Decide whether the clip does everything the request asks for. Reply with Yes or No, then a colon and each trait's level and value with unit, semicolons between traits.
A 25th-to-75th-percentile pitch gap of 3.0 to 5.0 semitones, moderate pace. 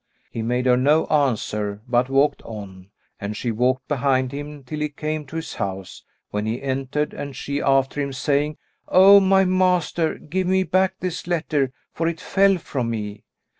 Yes: average, 4.6 semitones; average, 175 wpm